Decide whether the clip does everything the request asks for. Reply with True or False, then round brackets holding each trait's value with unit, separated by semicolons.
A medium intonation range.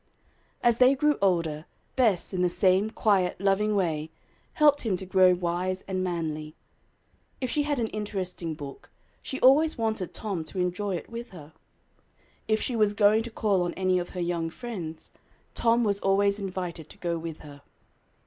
True (4.0 semitones)